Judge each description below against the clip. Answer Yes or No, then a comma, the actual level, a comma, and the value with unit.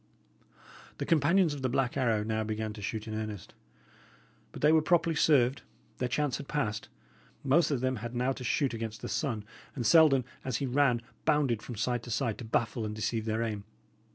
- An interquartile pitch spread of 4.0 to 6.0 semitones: Yes, average, 4.4 semitones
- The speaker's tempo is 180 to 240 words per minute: Yes, average, 200 wpm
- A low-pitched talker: Yes, low, 125 Hz